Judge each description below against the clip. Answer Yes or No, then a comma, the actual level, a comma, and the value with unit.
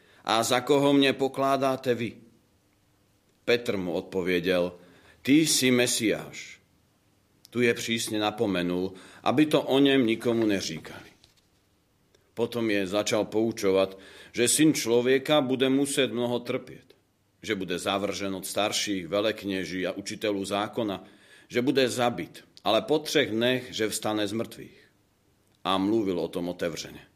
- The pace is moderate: Yes, average, 130 wpm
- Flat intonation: No, average, 4.3 semitones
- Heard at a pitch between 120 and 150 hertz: No, low, 110 Hz